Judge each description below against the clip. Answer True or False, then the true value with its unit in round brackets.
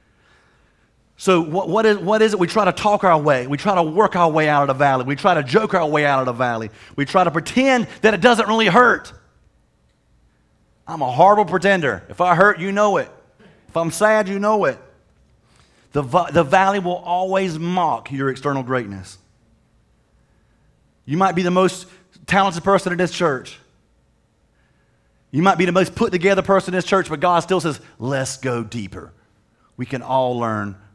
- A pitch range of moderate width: False (6.5 semitones)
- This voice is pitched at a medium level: True (175 Hz)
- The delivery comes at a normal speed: True (185 wpm)